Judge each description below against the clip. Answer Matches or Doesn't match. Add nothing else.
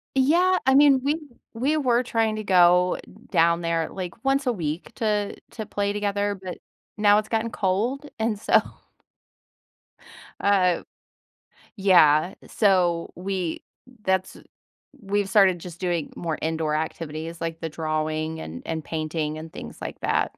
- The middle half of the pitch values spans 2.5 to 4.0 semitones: Doesn't match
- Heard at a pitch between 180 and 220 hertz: Matches